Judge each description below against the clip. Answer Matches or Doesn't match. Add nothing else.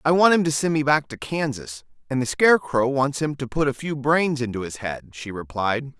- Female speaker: Doesn't match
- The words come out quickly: Matches